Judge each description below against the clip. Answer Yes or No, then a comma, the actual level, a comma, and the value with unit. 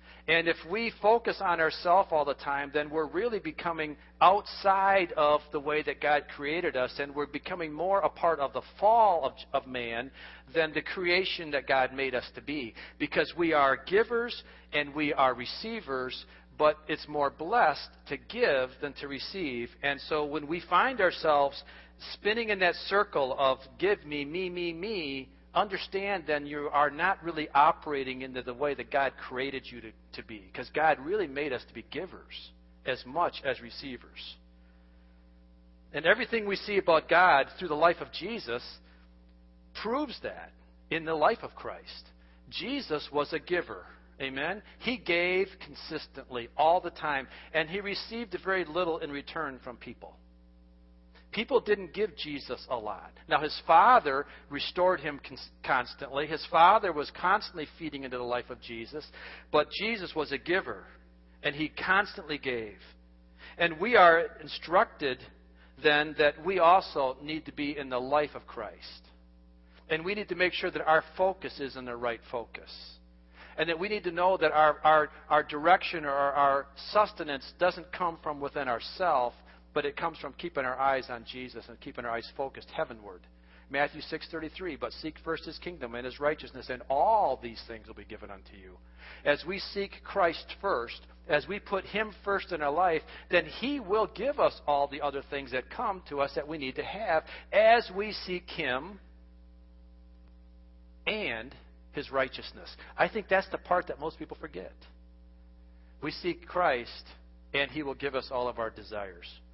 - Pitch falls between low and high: Yes, medium, 145 Hz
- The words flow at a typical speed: Yes, average, 175 wpm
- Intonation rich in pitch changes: Yes, wide, 7.3 semitones